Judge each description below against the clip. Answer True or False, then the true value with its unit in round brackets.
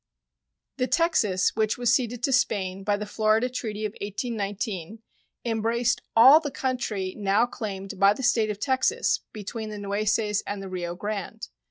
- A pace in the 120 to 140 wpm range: False (160 wpm)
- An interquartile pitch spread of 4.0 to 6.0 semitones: False (3.1 semitones)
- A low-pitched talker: False (215 Hz)